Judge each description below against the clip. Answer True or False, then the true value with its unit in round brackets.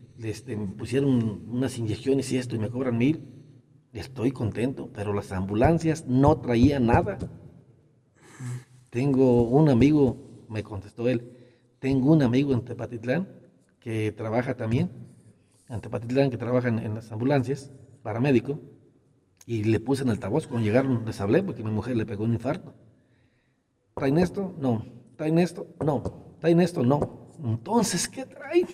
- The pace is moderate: True (150 wpm)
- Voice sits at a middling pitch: False (125 Hz)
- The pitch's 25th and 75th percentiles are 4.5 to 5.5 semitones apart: False (3.4 semitones)